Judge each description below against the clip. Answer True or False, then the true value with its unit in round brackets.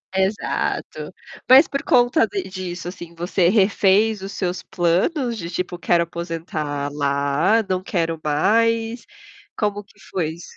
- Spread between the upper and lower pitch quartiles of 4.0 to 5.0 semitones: True (4.5 semitones)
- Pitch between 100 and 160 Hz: False (185 Hz)